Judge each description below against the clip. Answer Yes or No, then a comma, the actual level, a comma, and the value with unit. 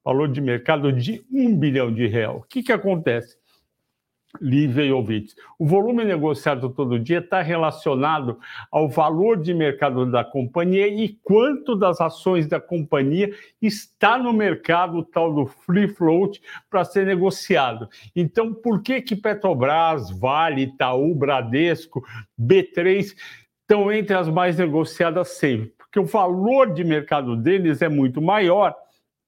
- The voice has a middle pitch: Yes, medium, 170 Hz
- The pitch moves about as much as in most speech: No, wide, 5.7 semitones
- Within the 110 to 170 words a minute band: Yes, average, 140 wpm